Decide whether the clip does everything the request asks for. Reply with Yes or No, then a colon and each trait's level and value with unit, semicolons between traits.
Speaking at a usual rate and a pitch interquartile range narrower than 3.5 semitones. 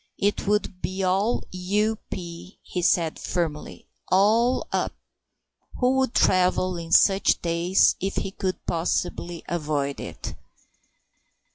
No: slow, 115 wpm; average, 2.9 semitones